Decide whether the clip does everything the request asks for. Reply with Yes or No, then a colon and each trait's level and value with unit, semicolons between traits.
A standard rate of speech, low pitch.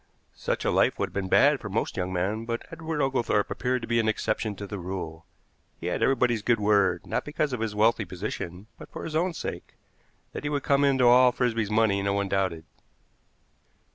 No: fast, 210 wpm; low, 110 Hz